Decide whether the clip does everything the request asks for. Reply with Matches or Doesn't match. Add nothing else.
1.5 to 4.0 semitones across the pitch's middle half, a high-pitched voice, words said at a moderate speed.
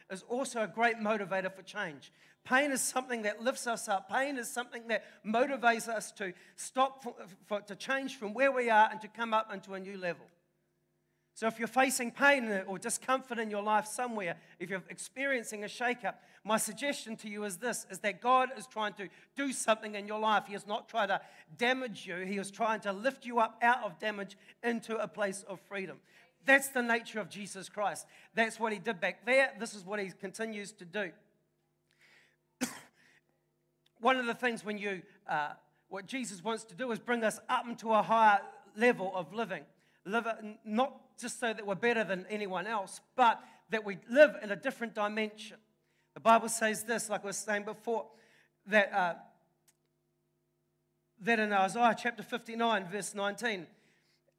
Matches